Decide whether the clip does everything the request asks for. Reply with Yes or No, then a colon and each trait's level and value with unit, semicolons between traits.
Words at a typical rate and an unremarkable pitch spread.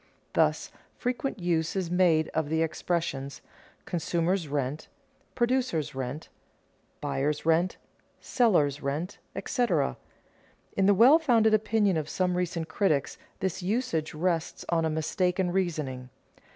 No: slow, 120 wpm; average, 4.0 semitones